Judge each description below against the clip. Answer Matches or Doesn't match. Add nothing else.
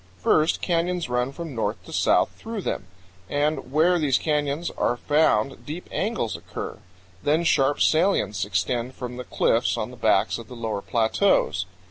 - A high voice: Doesn't match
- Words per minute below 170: Matches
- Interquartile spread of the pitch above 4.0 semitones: Matches